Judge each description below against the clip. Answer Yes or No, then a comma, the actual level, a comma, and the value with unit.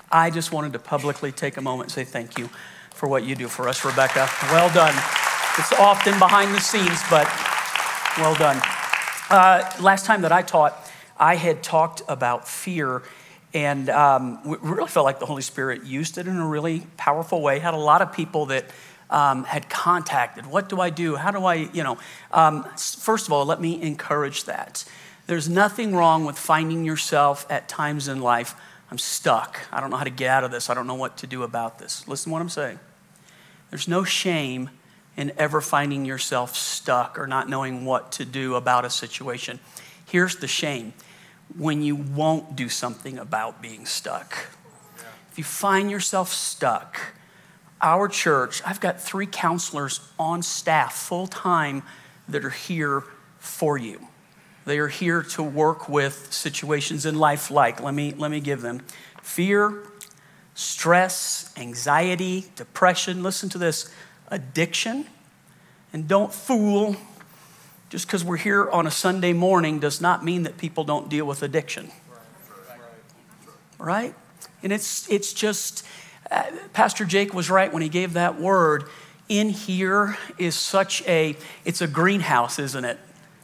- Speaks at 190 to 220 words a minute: No, average, 170 wpm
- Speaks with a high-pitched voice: No, medium, 160 Hz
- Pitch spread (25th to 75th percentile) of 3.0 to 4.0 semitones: No, average, 4.4 semitones